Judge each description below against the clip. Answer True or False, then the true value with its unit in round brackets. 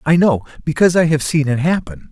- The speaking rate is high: True (225 wpm)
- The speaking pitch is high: False (150 Hz)